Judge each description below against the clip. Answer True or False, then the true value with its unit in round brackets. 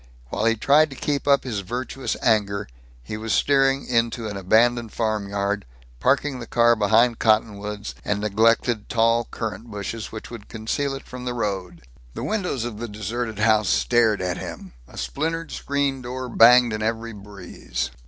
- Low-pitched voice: True (115 Hz)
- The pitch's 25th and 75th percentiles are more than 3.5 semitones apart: False (3.0 semitones)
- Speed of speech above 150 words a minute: True (165 wpm)